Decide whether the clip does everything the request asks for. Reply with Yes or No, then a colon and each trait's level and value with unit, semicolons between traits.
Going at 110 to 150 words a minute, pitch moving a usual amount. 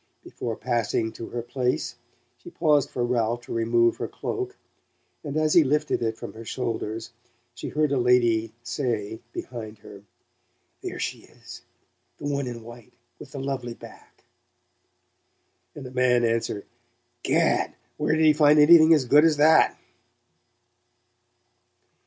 Yes: average, 145 wpm; average, 4.2 semitones